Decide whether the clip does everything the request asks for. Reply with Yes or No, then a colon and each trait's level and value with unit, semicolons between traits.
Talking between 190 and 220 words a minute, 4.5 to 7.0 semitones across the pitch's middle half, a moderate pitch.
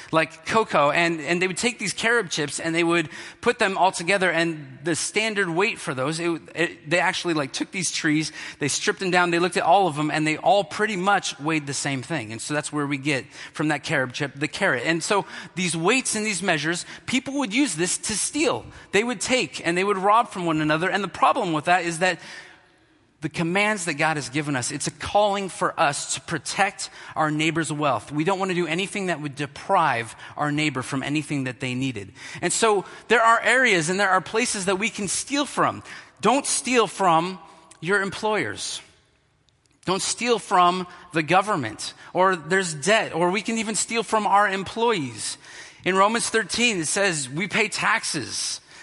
Yes: fast, 205 wpm; average, 4.8 semitones; medium, 175 Hz